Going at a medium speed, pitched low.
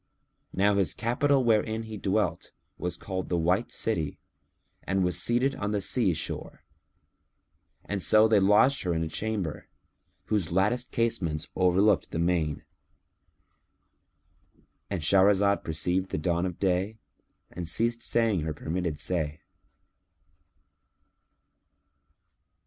No: slow, 115 wpm; very low, 95 Hz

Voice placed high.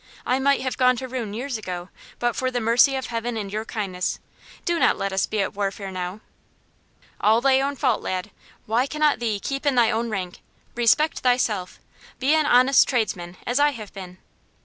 Yes: high, 235 Hz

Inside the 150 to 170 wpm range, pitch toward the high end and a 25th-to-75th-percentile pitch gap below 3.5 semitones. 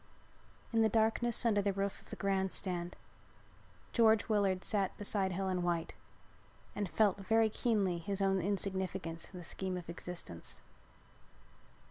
No: average, 140 wpm; high, 195 Hz; narrow, 2.4 semitones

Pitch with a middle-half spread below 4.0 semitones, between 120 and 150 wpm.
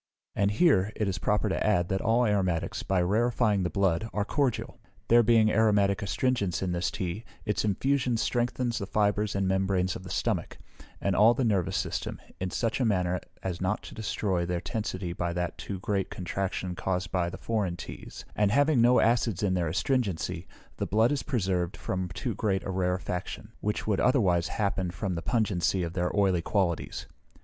No: average, 3.4 semitones; average, 185 wpm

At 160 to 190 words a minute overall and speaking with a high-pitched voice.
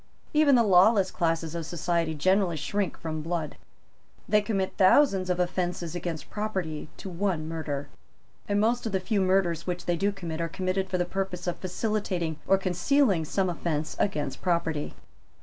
No: average, 165 wpm; medium, 180 Hz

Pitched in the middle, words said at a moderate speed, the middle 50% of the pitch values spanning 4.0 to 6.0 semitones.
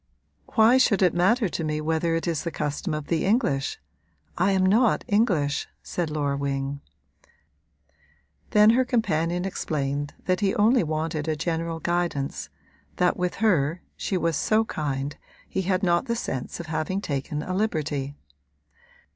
Yes: medium, 170 Hz; average, 155 wpm; average, 4.4 semitones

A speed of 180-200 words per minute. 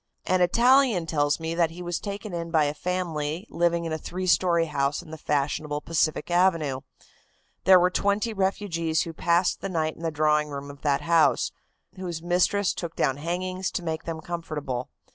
Yes: average, 185 wpm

